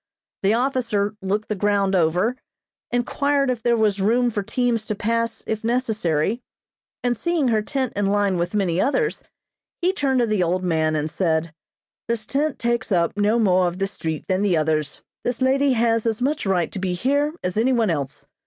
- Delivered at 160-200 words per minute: Yes, average, 190 wpm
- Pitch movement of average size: Yes, average, 4.9 semitones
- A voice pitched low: No, high, 215 Hz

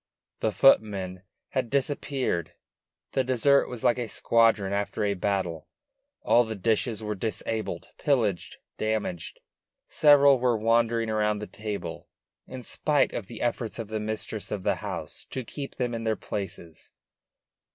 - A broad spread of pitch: No, average, 3.1 semitones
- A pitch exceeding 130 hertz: No, low, 110 Hz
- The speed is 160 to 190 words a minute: No, average, 145 wpm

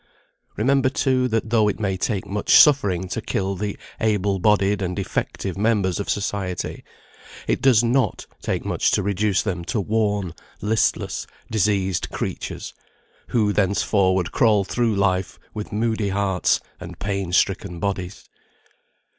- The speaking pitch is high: No, low, 100 Hz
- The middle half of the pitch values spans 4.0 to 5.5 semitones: No, narrow, 2.5 semitones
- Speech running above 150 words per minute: No, average, 140 wpm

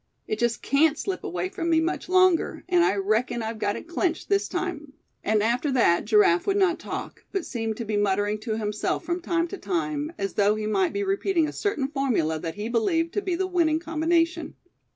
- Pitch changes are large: Yes, wide, 8.2 semitones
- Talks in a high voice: Yes, very high, 300 Hz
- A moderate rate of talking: No, fast, 215 wpm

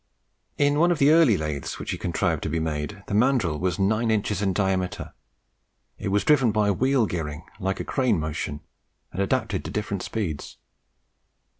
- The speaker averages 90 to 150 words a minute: No, average, 170 wpm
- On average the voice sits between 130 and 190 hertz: No, low, 100 Hz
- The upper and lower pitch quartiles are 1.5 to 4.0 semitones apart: No, average, 5.2 semitones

